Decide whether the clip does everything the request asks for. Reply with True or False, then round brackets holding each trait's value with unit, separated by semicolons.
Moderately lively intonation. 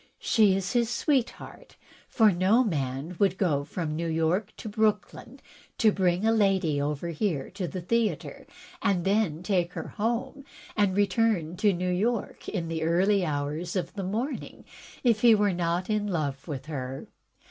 True (4.6 semitones)